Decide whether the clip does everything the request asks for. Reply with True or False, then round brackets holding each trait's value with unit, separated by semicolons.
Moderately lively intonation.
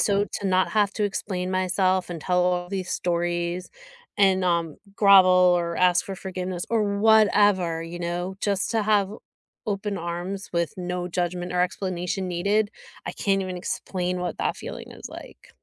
False (2.0 semitones)